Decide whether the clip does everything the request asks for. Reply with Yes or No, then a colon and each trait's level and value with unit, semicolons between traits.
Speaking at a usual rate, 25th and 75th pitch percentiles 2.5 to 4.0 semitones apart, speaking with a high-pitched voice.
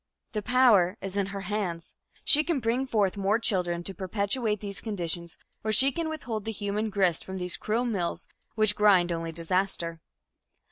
Yes: average, 175 wpm; average, 3.6 semitones; high, 200 Hz